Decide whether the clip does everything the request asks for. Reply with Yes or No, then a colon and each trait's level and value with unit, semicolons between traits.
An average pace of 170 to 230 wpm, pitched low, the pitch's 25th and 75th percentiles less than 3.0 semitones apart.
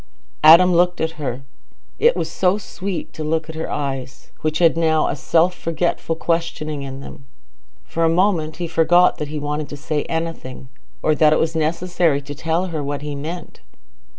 No: average, 180 wpm; medium, 160 Hz; narrow, 2.5 semitones